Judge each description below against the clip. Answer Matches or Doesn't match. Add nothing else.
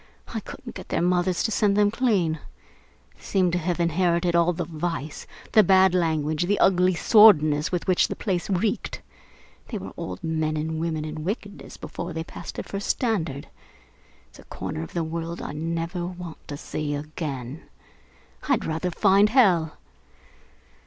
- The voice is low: Doesn't match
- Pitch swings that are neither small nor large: Matches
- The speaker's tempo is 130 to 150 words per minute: Doesn't match